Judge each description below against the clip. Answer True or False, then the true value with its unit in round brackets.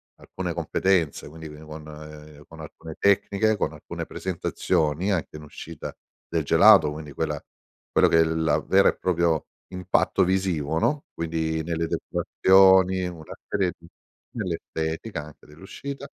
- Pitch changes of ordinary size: True (3.4 semitones)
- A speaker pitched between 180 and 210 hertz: False (80 Hz)